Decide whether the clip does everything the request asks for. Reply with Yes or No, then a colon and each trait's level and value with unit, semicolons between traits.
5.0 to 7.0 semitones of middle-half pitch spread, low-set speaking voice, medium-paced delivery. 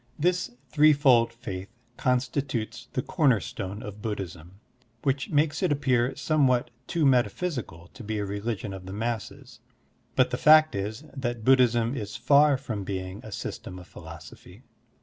Yes: wide, 5.4 semitones; low, 120 Hz; average, 150 wpm